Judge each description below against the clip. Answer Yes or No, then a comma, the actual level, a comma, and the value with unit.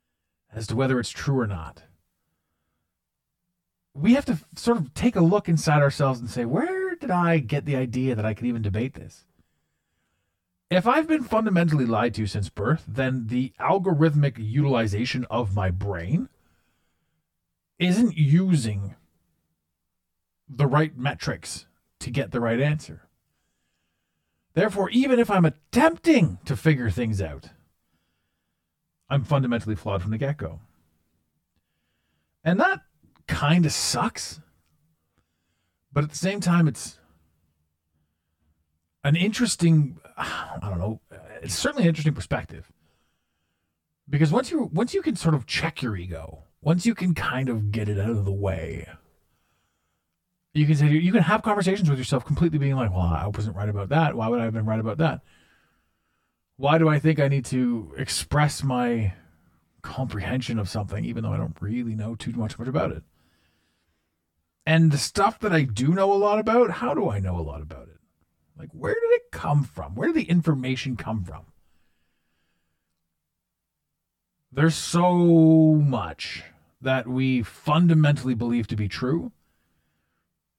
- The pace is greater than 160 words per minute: No, average, 150 wpm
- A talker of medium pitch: No, low, 105 Hz